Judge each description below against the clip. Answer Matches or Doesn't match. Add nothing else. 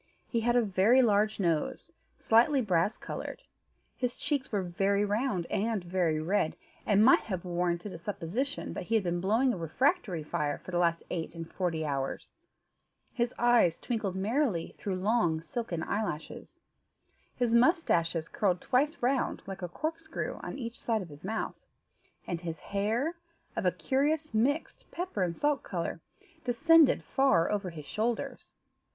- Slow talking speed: Doesn't match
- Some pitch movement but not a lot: Doesn't match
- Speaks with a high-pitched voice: Matches